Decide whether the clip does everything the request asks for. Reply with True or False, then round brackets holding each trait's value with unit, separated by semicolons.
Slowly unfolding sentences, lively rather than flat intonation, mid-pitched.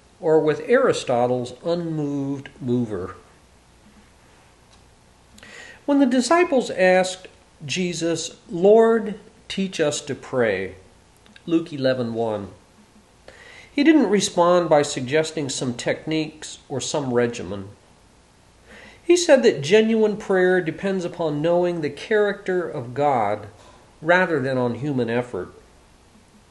True (100 wpm; 7.3 semitones; 155 Hz)